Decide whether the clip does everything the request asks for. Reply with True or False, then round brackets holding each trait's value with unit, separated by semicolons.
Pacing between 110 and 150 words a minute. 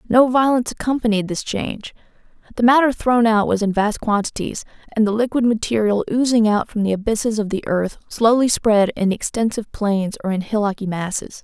False (180 wpm)